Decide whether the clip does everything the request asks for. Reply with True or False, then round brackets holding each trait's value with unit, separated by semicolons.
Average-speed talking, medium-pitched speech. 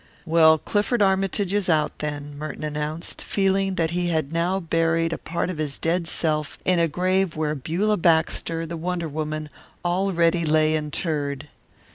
True (160 wpm; 165 Hz)